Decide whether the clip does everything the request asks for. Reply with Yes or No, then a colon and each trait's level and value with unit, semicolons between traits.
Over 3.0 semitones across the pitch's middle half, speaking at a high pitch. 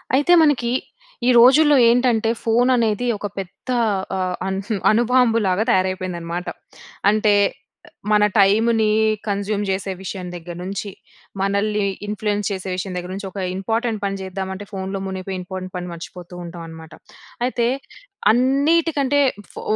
Yes: average, 3.7 semitones; high, 200 Hz